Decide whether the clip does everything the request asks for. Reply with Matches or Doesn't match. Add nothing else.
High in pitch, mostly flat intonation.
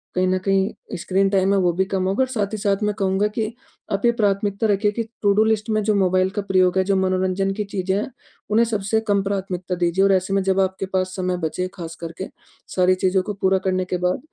Matches